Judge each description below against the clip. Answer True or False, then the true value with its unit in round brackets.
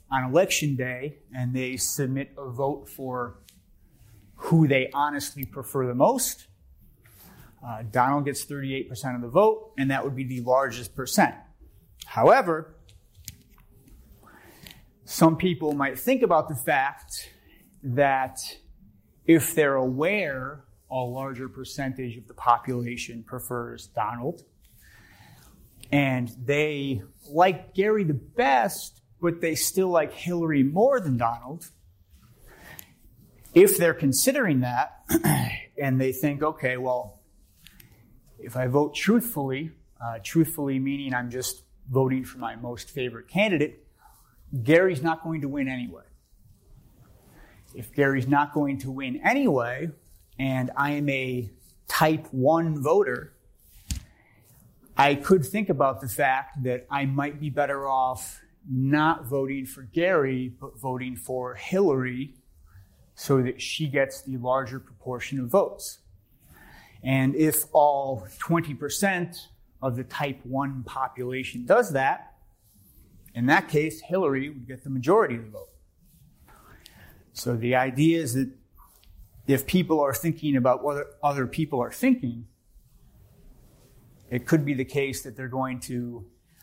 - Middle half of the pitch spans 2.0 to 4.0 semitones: True (3.0 semitones)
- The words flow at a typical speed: False (125 wpm)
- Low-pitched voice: True (130 Hz)